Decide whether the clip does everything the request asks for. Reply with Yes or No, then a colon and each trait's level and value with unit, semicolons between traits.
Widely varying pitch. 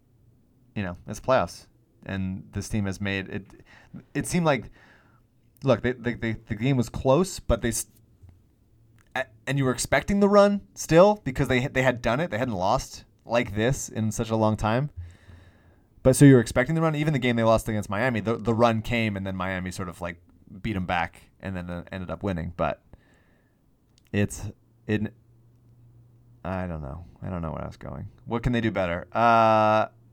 No: average, 3.8 semitones